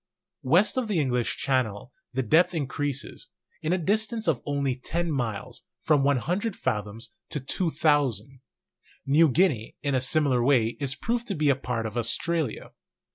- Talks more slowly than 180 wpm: Yes, average, 155 wpm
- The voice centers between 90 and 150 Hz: Yes, medium, 140 Hz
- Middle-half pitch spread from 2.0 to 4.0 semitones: No, average, 5.1 semitones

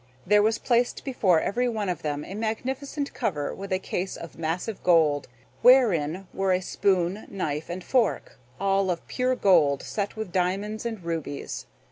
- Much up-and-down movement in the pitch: No, average, 4.5 semitones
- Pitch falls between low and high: No, high, 195 Hz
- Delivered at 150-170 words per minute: Yes, average, 165 wpm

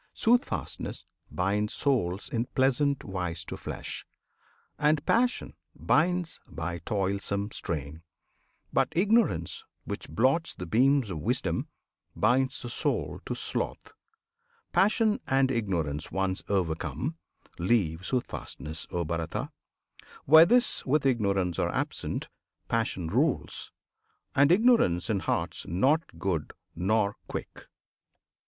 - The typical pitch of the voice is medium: No, low, 105 Hz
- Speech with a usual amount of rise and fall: No, wide, 8.4 semitones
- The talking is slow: Yes, slow, 110 wpm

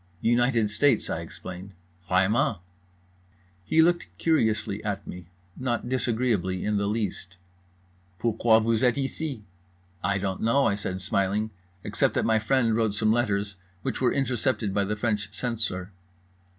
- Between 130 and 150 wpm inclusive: Yes, average, 140 wpm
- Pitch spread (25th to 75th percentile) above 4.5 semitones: No, average, 4.1 semitones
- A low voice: Yes, low, 105 Hz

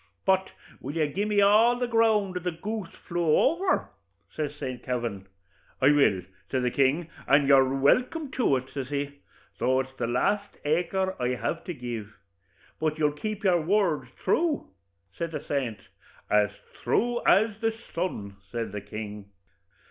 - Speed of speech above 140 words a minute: Yes, average, 160 wpm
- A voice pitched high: No, medium, 155 Hz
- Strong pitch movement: Yes, wide, 7.7 semitones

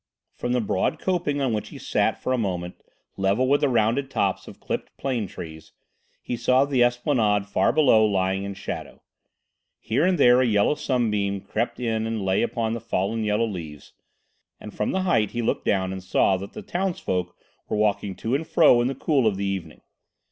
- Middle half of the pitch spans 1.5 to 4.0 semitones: No, average, 4.5 semitones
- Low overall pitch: Yes, low, 110 Hz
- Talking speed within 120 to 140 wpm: No, average, 200 wpm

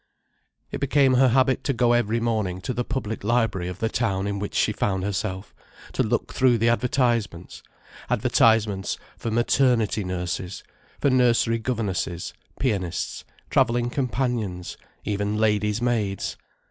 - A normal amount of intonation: Yes, average, 3.5 semitones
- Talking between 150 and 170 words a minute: No, slow, 135 wpm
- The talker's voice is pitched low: Yes, low, 115 Hz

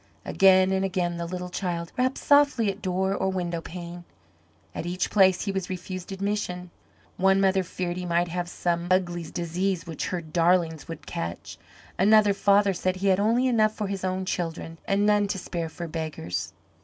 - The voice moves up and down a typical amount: No, narrow, 2.2 semitones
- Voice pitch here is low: No, medium, 185 Hz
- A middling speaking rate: Yes, average, 180 wpm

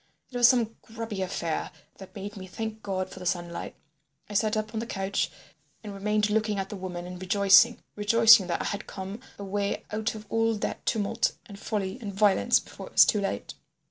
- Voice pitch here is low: No, high, 205 Hz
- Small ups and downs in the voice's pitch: Yes, narrow, 2.3 semitones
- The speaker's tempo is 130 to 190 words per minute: No, average, 200 wpm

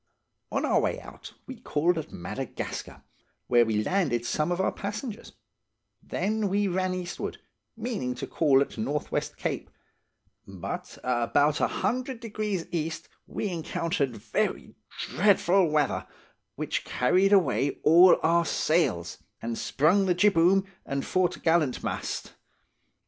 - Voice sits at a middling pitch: Yes, medium, 170 Hz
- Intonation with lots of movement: Yes, wide, 5.8 semitones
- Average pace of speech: No, slow, 125 wpm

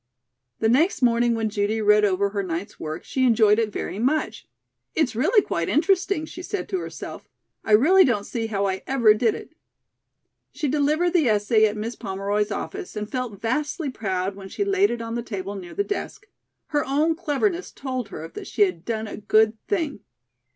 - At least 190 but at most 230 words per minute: Yes, average, 195 wpm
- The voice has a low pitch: No, high, 230 Hz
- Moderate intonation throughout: No, wide, 6.6 semitones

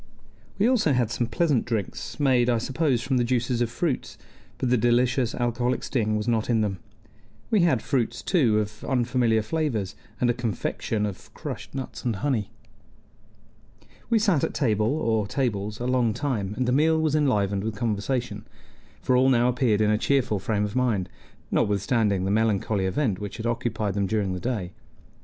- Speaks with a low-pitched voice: Yes, low, 120 Hz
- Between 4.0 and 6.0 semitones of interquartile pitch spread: No, average, 3.4 semitones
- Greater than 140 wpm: Yes, average, 180 wpm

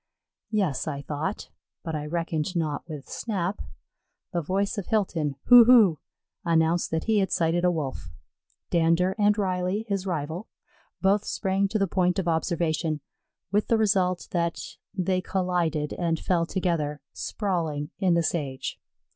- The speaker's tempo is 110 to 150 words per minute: Yes, average, 145 wpm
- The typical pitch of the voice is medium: Yes, medium, 175 Hz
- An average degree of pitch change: Yes, average, 3.3 semitones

